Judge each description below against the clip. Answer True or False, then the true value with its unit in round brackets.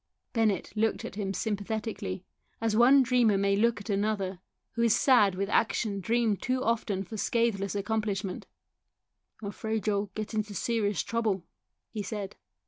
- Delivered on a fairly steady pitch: True (2.3 semitones)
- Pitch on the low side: False (210 Hz)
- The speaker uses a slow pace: False (155 wpm)